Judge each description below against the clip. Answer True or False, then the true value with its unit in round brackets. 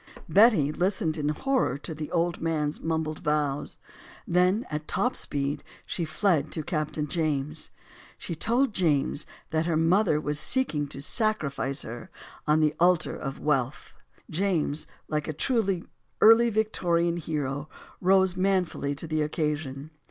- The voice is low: False (155 Hz)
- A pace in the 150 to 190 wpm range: False (140 wpm)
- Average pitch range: True (3.6 semitones)